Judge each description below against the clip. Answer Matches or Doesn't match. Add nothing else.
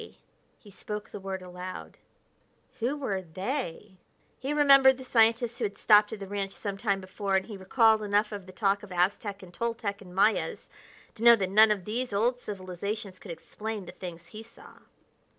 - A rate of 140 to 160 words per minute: Doesn't match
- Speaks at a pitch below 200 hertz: Doesn't match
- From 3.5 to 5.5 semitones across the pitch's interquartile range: Doesn't match